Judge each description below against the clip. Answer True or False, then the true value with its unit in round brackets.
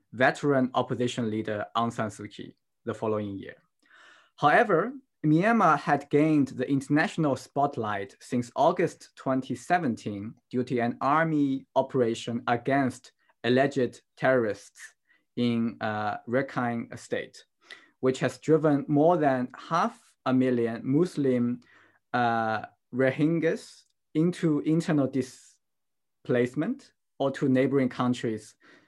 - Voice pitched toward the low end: True (130 Hz)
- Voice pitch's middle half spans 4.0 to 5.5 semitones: False (3.5 semitones)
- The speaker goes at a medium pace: False (105 wpm)